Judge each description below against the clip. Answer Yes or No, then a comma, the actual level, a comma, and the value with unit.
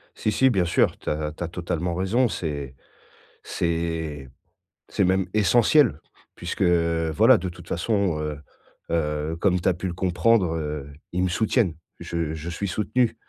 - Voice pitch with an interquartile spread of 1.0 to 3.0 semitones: No, average, 3.4 semitones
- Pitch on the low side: Yes, very low, 85 Hz